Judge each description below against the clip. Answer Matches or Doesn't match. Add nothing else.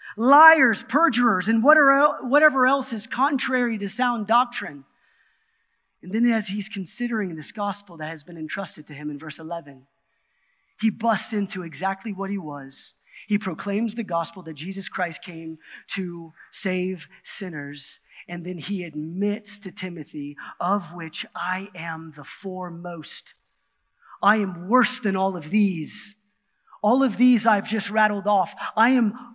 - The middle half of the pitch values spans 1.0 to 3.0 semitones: Doesn't match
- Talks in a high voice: Matches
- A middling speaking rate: Matches